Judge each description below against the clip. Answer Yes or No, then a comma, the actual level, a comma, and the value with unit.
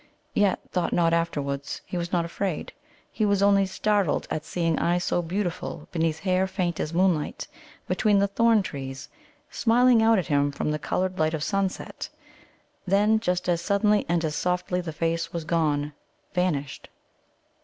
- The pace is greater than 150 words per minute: Yes, average, 165 wpm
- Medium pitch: Yes, medium, 175 Hz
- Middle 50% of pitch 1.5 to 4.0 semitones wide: Yes, average, 3.5 semitones